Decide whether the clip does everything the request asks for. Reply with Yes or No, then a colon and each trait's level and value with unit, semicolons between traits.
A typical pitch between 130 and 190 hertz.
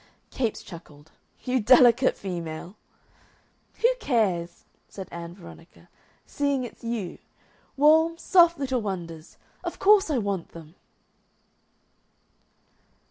No: high, 220 Hz